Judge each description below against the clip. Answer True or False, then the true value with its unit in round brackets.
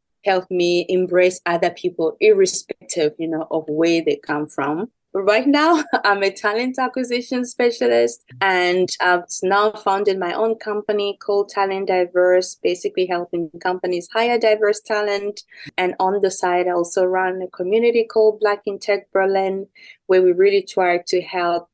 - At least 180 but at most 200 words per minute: False (155 wpm)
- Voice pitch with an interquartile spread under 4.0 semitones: True (2.7 semitones)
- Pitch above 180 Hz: True (190 Hz)